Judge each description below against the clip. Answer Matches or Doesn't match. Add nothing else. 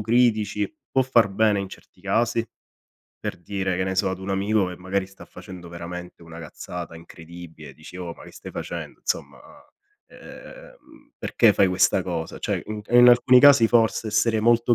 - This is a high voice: Doesn't match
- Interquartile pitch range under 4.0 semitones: Doesn't match